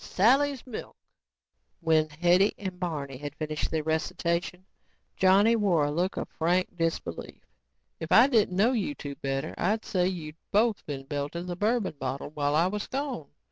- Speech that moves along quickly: No, average, 155 wpm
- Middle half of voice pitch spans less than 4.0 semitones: No, average, 4.5 semitones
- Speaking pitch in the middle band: Yes, medium, 175 Hz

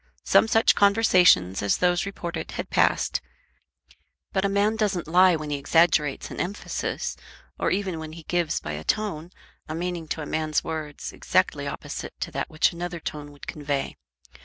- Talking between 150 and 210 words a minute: Yes, average, 170 wpm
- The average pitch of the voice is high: No, medium, 170 Hz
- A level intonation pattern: No, average, 3.7 semitones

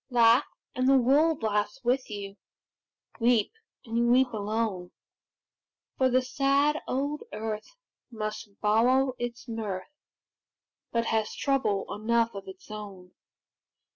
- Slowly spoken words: Yes, slow, 120 wpm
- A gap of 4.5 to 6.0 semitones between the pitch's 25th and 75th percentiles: No, average, 3.5 semitones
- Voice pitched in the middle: No, high, 230 Hz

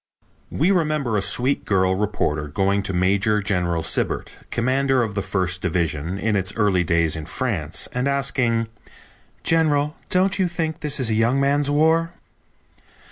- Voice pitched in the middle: No, low, 110 Hz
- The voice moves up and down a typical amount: No, wide, 7.2 semitones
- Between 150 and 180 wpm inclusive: Yes, average, 155 wpm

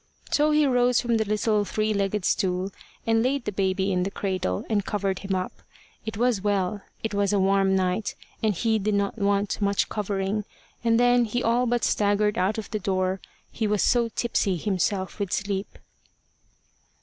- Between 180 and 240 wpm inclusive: Yes, average, 185 wpm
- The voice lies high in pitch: Yes, high, 205 Hz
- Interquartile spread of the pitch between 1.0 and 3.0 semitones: Yes, narrow, 2.6 semitones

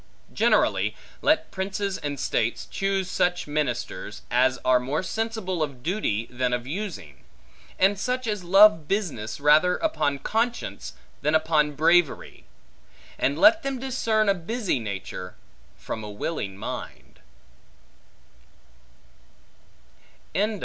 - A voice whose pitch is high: No, medium, 165 Hz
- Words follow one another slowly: Yes, slow, 115 wpm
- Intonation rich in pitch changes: Yes, wide, 8.0 semitones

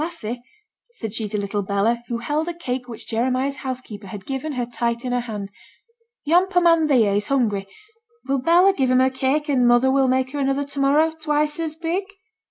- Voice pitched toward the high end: Yes, very high, 260 Hz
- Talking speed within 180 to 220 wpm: Yes, fast, 205 wpm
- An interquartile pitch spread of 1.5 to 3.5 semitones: No, average, 4.3 semitones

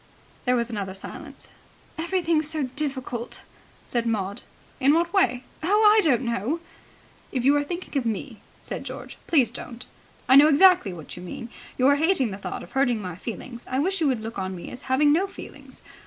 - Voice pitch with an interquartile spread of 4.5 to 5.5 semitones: Yes, average, 5.2 semitones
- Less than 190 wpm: No, average, 195 wpm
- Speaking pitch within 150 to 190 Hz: No, very high, 260 Hz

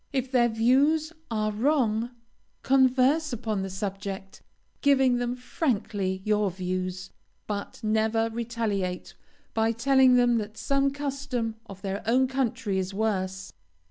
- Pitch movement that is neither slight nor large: Yes, average, 4.4 semitones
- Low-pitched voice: No, high, 225 Hz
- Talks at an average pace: No, slow, 125 wpm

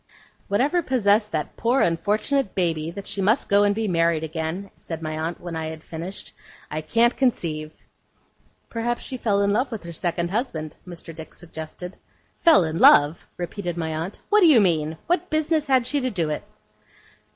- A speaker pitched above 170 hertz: Yes, medium, 185 Hz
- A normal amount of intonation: No, wide, 6.6 semitones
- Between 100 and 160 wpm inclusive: No, average, 185 wpm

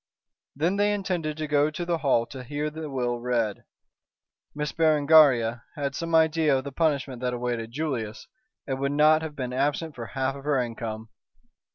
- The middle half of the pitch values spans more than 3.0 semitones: Yes, average, 4.0 semitones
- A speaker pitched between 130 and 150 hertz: Yes, medium, 140 Hz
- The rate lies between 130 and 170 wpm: No, average, 180 wpm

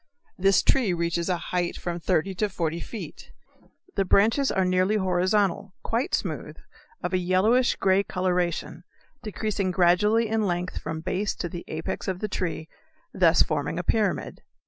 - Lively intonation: No, average, 2.9 semitones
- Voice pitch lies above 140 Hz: Yes, medium, 185 Hz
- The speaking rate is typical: Yes, average, 160 wpm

